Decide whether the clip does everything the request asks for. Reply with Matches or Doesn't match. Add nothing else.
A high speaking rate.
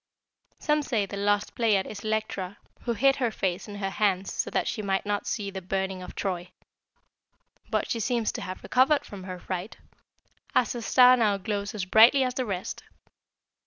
Doesn't match